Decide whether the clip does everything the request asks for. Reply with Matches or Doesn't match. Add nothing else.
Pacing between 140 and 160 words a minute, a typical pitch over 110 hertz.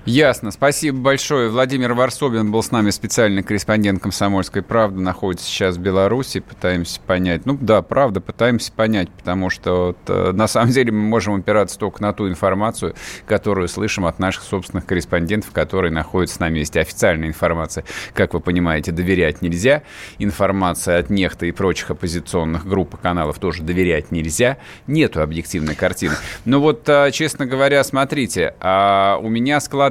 Doesn't match